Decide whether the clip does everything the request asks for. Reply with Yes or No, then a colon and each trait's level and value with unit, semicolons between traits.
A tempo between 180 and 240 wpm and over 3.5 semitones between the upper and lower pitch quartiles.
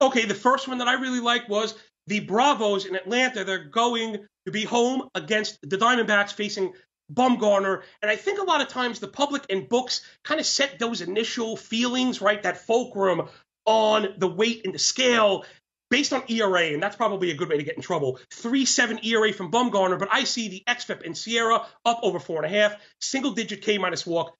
Yes: average, 200 wpm; average, 4.0 semitones